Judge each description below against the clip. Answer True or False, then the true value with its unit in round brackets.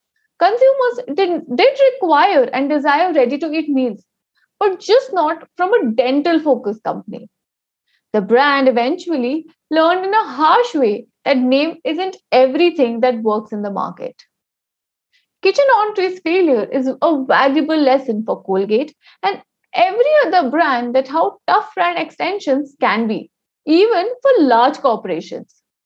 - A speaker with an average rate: False (130 wpm)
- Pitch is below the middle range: False (310 Hz)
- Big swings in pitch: True (6.3 semitones)